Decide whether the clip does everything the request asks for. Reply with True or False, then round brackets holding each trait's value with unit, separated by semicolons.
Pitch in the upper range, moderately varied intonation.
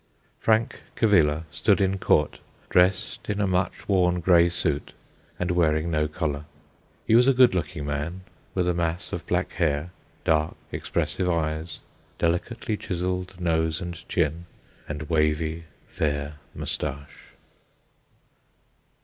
False (85 Hz; 3.0 semitones)